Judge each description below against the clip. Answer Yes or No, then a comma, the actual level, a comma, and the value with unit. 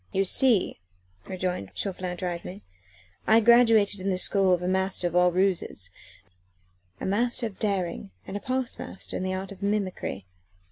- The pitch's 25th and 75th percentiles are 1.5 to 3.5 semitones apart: Yes, narrow, 2.4 semitones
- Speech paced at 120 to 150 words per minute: No, average, 160 wpm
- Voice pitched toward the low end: No, high, 190 Hz